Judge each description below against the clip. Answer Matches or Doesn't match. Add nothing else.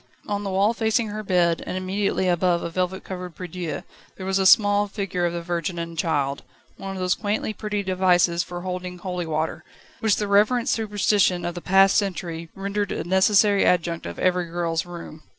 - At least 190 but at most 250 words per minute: Matches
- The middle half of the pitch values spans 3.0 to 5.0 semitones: Doesn't match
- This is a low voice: Doesn't match